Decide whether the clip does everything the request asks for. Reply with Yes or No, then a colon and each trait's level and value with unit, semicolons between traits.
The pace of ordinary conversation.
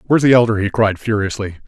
No: fast, 215 wpm